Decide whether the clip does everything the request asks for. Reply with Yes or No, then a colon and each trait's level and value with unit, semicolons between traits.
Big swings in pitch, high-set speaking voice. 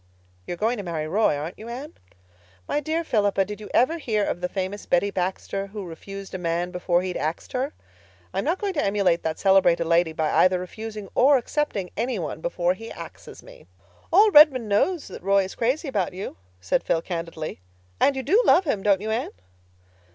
Yes: wide, 5.9 semitones; high, 200 Hz